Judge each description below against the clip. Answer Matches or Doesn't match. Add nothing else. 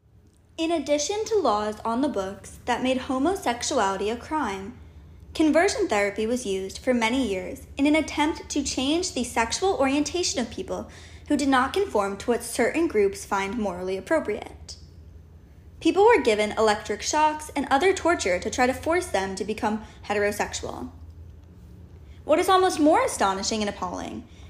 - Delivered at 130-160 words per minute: Matches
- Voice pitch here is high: Matches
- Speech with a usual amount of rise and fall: Doesn't match